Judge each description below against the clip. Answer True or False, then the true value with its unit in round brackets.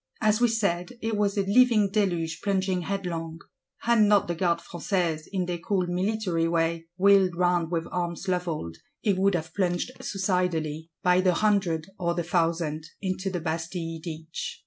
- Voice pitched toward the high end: False (180 Hz)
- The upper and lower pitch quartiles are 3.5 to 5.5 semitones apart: False (3.0 semitones)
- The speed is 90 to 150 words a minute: False (165 wpm)